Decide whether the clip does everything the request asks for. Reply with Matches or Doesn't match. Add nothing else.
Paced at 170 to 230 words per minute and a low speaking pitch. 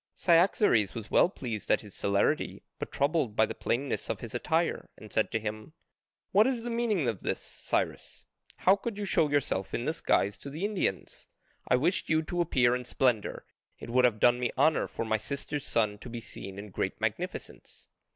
Matches